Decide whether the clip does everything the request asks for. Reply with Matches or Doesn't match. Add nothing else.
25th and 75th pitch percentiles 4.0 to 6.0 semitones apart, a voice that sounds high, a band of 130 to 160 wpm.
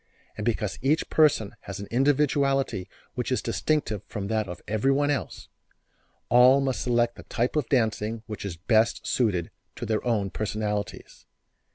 Doesn't match